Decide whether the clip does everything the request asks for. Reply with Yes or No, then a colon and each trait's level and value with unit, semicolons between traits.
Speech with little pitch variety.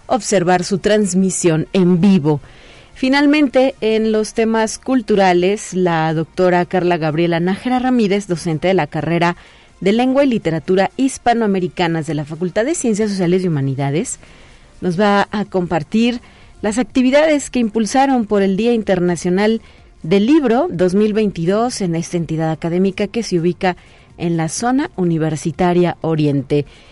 No: average, 4.4 semitones